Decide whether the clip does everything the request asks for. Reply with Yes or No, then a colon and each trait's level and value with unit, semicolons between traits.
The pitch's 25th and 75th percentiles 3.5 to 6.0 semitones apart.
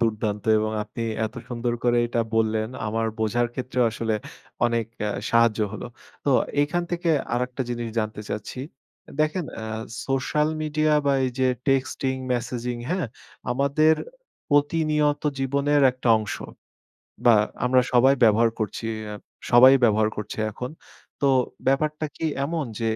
Yes: average, 4.2 semitones